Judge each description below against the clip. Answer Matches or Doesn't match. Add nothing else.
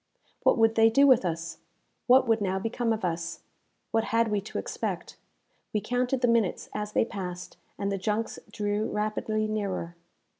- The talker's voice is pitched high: Matches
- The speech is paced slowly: Doesn't match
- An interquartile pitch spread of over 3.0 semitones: Doesn't match